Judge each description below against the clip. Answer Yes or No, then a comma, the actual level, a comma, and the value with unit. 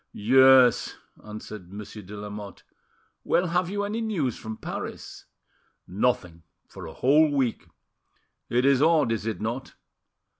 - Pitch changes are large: Yes, wide, 5.8 semitones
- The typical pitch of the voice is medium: No, low, 125 Hz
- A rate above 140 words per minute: No, slow, 135 wpm